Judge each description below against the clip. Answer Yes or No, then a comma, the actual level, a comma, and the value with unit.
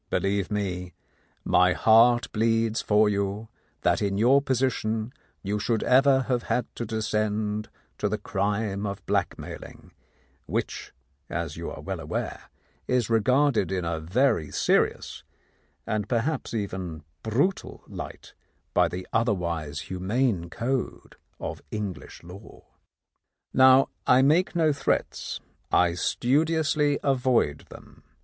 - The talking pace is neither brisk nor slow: No, slow, 125 wpm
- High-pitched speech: No, low, 110 Hz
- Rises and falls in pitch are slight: No, average, 4.6 semitones